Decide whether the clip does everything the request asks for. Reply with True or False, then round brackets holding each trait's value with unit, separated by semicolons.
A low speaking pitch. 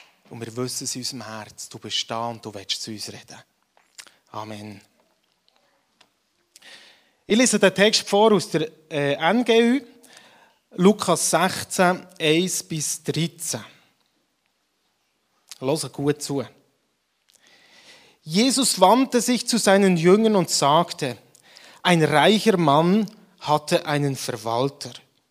False (160 Hz)